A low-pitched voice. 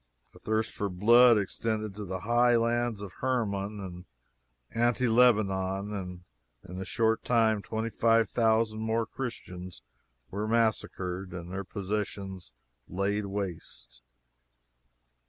Yes: low, 105 Hz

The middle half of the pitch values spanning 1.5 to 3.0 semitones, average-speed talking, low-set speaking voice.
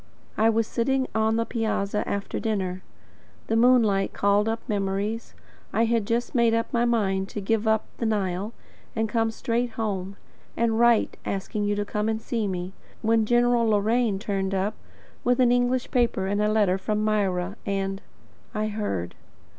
No: narrow, 2.5 semitones; average, 170 wpm; high, 215 Hz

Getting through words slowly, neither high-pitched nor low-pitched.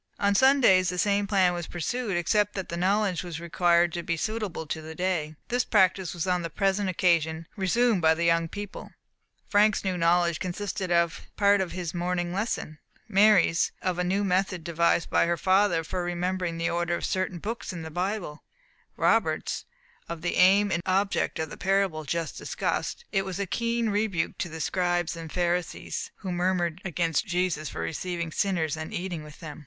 No: average, 185 wpm; medium, 180 Hz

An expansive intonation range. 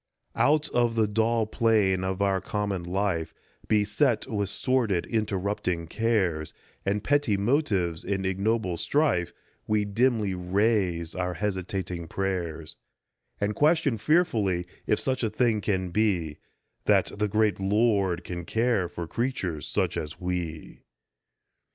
No: average, 3.8 semitones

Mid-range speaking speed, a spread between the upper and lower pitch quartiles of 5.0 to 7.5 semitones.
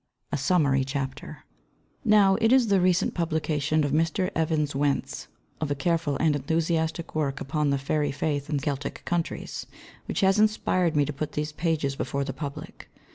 No: average, 170 wpm; average, 2.9 semitones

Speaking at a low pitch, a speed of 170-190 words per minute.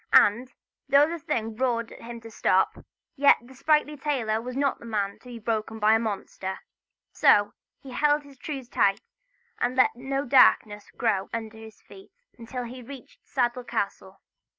No: high, 240 Hz; average, 175 wpm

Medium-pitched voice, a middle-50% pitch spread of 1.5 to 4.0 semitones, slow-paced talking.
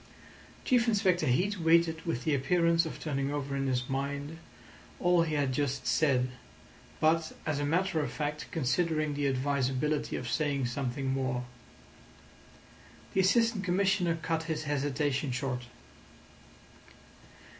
Yes: medium, 150 Hz; average, 3.6 semitones; slow, 130 wpm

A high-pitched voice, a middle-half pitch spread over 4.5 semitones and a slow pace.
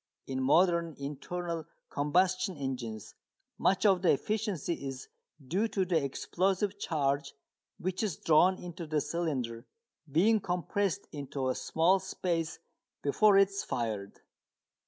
No: medium, 170 Hz; average, 5.2 semitones; slow, 125 wpm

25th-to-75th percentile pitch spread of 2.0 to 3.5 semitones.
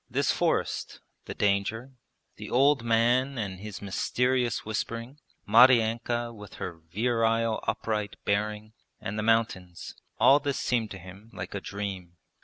Yes: average, 2.9 semitones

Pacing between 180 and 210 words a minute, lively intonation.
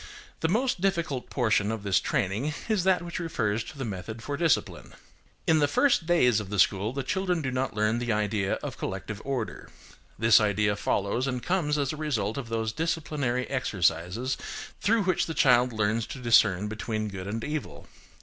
Yes: average, 185 wpm; wide, 6.2 semitones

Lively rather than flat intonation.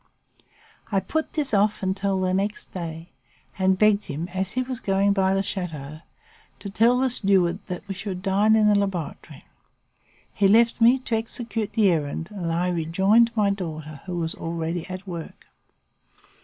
No: average, 3.3 semitones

